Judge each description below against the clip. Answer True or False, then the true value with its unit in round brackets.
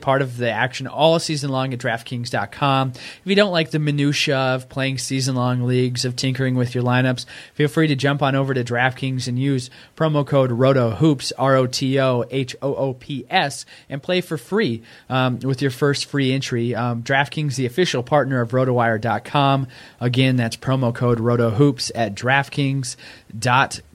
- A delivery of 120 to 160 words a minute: False (175 wpm)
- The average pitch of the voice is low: True (130 Hz)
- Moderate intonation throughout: False (2.1 semitones)